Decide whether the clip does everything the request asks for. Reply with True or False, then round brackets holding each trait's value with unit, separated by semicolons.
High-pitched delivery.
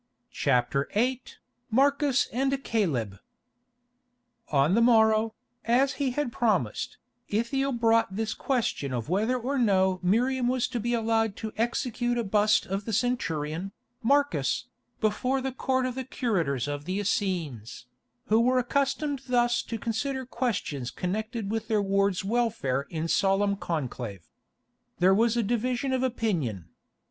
True (225 Hz)